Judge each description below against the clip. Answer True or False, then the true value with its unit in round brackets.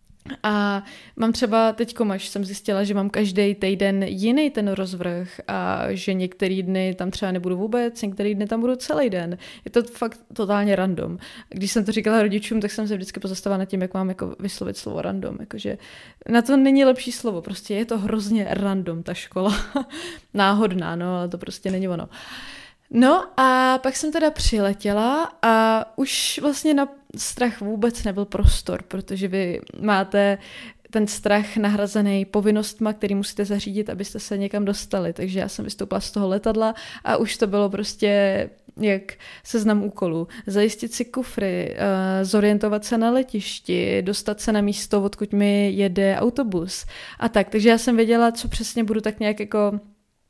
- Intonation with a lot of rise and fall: False (2.6 semitones)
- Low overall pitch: False (210 Hz)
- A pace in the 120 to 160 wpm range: False (170 wpm)